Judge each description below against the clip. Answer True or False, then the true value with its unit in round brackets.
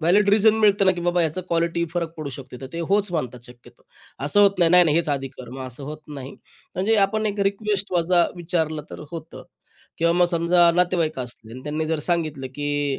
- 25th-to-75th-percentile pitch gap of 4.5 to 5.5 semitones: False (3.9 semitones)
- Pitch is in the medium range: True (170 Hz)